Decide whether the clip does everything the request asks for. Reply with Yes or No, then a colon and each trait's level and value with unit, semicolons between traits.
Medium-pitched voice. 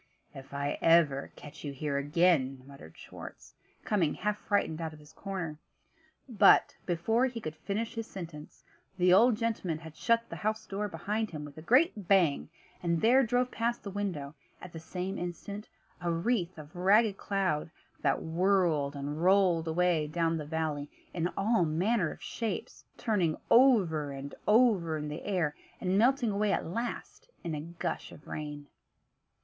Yes: medium, 175 Hz